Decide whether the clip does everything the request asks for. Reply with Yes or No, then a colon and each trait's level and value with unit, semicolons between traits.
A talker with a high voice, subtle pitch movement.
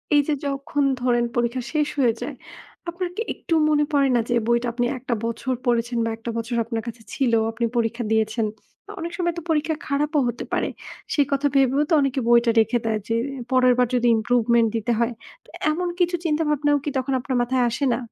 No: very high, 250 Hz; average, 3.7 semitones